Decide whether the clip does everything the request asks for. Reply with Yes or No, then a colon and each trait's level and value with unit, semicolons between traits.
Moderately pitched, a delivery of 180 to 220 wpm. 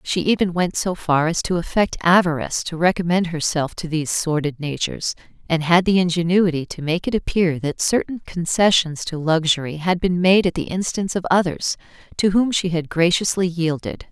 Yes: medium, 170 Hz; average, 185 wpm